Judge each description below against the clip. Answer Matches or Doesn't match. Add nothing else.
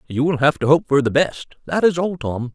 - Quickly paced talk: Matches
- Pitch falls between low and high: Matches